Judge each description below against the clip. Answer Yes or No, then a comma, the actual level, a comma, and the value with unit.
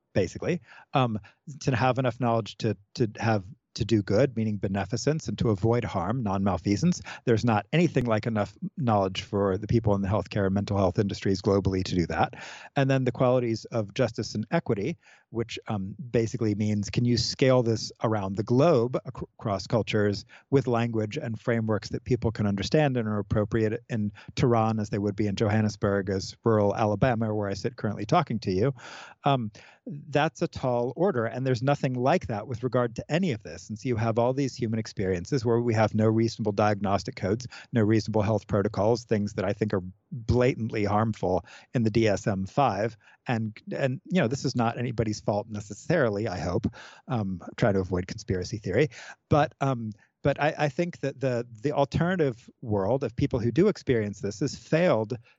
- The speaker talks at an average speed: Yes, average, 190 wpm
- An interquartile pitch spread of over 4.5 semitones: No, average, 3.7 semitones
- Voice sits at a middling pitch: No, low, 115 Hz